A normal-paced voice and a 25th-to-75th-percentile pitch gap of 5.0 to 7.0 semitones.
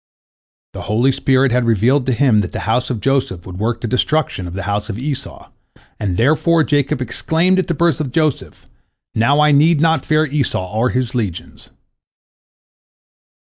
Yes: average, 175 wpm; average, 5.3 semitones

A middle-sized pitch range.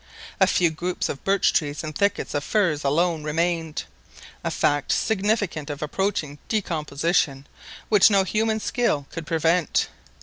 Yes: average, 4.7 semitones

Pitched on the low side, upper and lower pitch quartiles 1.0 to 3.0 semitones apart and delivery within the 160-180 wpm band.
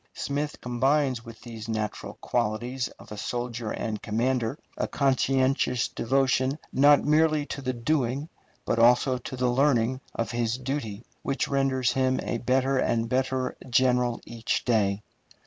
No: low, 125 Hz; narrow, 2.4 semitones; average, 145 wpm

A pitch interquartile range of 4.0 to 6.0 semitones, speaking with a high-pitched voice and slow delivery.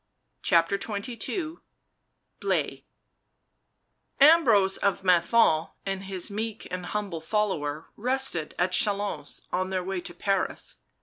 No: average, 3.0 semitones; high, 195 Hz; slow, 110 wpm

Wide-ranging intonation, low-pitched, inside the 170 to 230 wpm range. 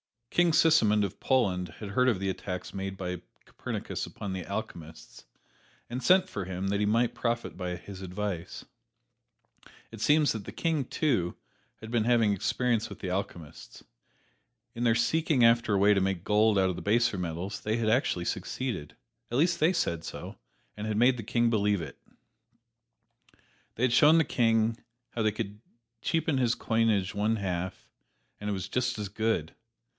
No: average, 3.9 semitones; low, 105 Hz; average, 175 wpm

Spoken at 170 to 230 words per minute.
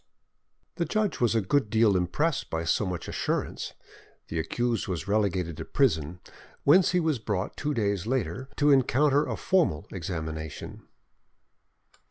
No: average, 145 wpm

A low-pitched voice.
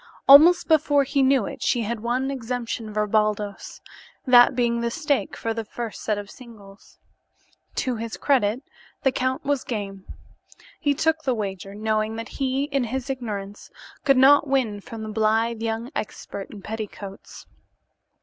No: high, 230 Hz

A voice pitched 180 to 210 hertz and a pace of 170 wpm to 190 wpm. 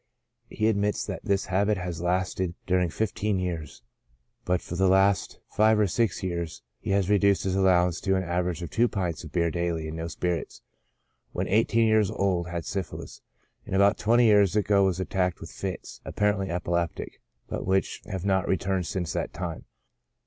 No: very low, 95 Hz; average, 180 wpm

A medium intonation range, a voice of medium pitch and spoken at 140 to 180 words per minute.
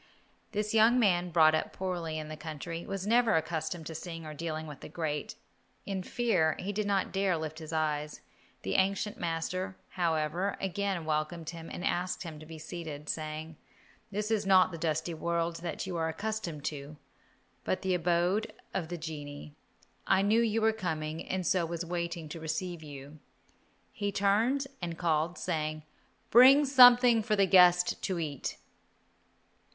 Yes: average, 3.8 semitones; medium, 170 Hz; average, 170 wpm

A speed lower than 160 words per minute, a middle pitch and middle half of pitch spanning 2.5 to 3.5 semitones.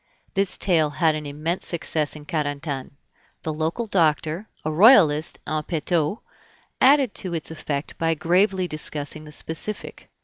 Yes: average, 140 wpm; medium, 160 Hz; average, 3.2 semitones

